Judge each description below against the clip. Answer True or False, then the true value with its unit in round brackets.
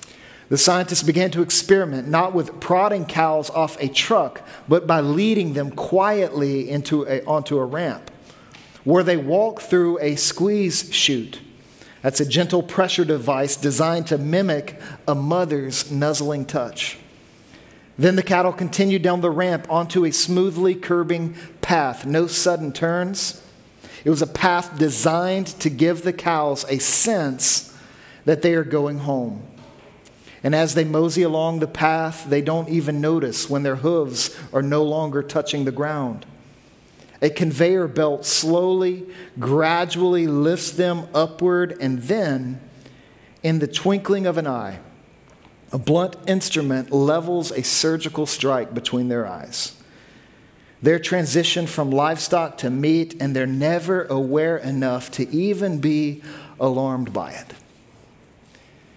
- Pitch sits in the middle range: True (160 Hz)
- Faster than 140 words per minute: False (135 wpm)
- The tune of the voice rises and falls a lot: False (3.7 semitones)